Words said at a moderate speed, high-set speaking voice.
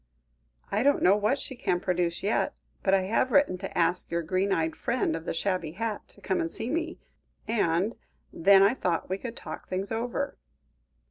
Yes: average, 195 wpm; high, 195 Hz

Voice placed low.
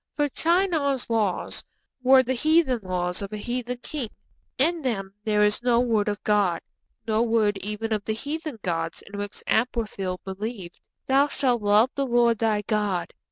No: high, 225 Hz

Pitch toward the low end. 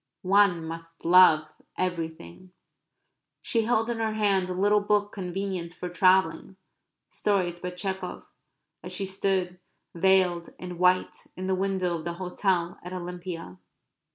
No: medium, 185 Hz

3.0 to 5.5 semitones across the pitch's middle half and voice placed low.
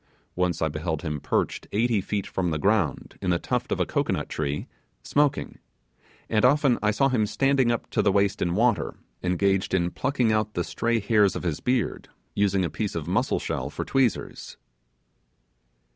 Yes: average, 5.0 semitones; low, 100 Hz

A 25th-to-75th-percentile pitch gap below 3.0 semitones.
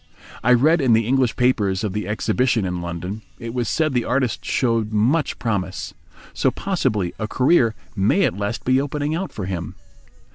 No: average, 4.3 semitones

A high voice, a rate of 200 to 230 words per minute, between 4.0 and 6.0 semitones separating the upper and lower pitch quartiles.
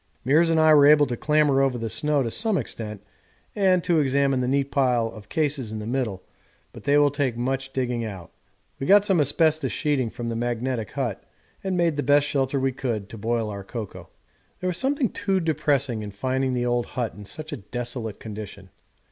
No: low, 130 Hz; fast, 205 wpm; average, 4.4 semitones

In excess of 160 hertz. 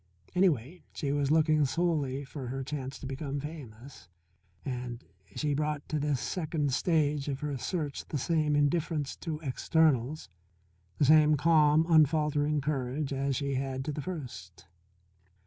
No: medium, 145 Hz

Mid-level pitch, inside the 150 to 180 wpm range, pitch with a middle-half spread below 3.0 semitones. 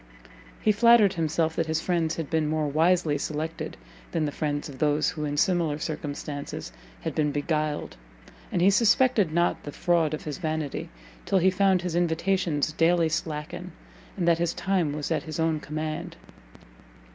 Yes: medium, 160 Hz; average, 170 wpm; narrow, 2.6 semitones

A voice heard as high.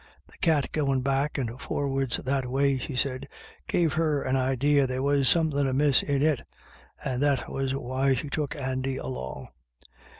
No: low, 135 Hz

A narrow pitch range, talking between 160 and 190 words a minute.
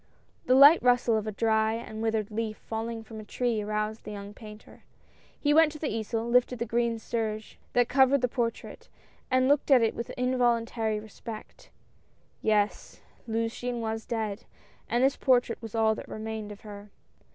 Yes: narrow, 2.2 semitones; average, 175 wpm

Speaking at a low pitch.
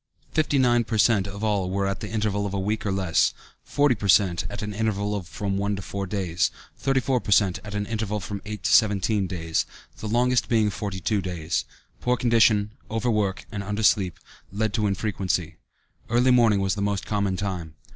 Yes: low, 105 Hz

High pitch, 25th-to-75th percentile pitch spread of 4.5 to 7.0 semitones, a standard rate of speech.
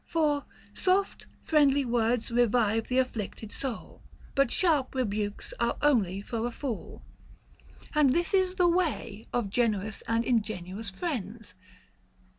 No: high, 240 Hz; average, 5.1 semitones; slow, 125 wpm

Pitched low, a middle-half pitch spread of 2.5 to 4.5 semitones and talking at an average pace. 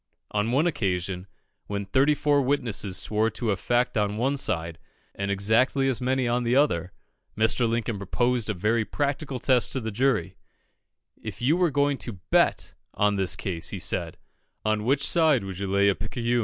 No: low, 115 Hz; average, 5.0 semitones; average, 185 wpm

